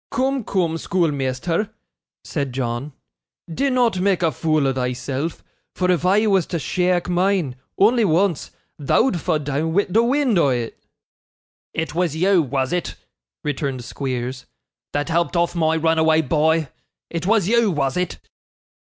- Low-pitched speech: No, medium, 165 Hz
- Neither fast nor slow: Yes, average, 145 wpm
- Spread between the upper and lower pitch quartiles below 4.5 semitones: No, average, 4.8 semitones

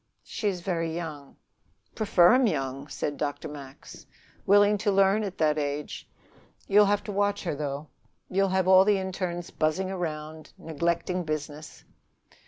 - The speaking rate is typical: Yes, average, 150 wpm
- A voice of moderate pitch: Yes, medium, 175 Hz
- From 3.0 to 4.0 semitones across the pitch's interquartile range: No, average, 4.4 semitones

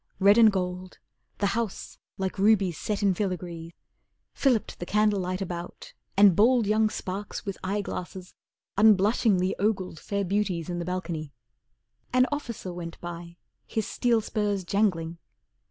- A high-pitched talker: Yes, high, 195 Hz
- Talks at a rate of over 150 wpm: No, average, 140 wpm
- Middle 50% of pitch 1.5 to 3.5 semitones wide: Yes, average, 2.9 semitones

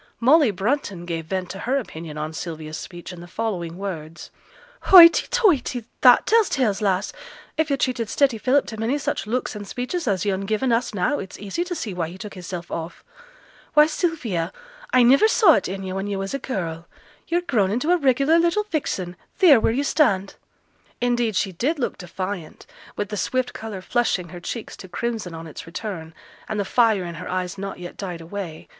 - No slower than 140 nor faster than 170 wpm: No, average, 200 wpm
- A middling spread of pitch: No, wide, 6.3 semitones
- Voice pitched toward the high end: Yes, high, 205 Hz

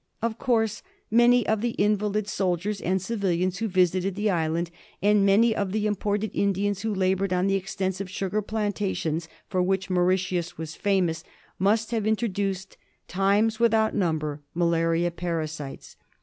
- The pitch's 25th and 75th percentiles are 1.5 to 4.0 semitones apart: Yes, average, 2.9 semitones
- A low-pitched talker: No, high, 195 Hz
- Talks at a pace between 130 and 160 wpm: Yes, average, 145 wpm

